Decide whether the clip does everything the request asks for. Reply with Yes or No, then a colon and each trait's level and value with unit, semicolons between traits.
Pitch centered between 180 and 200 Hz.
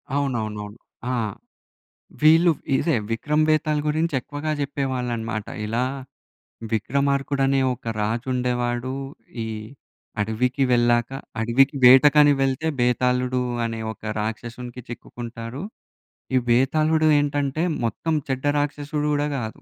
No: low, 130 Hz